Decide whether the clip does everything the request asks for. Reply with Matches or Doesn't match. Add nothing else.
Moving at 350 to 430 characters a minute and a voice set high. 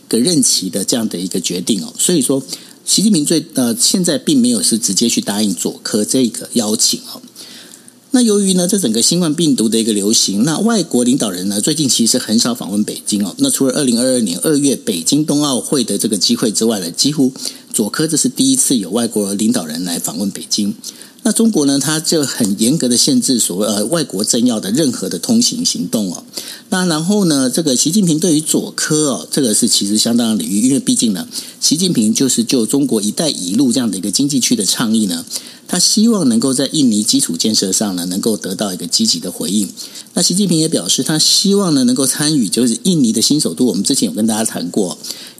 Doesn't match